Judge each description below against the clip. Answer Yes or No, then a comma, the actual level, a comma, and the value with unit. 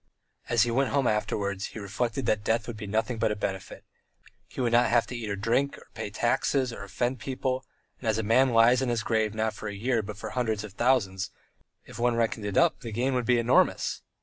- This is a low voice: Yes, low, 115 Hz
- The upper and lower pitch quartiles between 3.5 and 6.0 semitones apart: No, narrow, 2.6 semitones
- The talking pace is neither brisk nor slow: No, fast, 235 wpm